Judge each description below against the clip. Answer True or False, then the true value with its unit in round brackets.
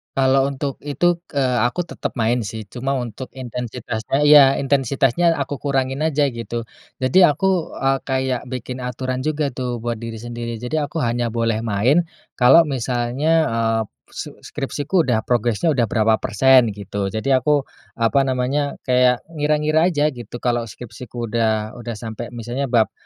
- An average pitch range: True (3.2 semitones)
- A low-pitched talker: True (125 Hz)